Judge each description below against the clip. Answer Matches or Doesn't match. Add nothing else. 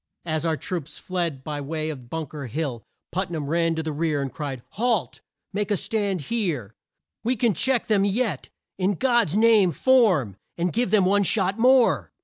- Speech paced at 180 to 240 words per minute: Matches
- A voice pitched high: Doesn't match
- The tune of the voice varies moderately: Doesn't match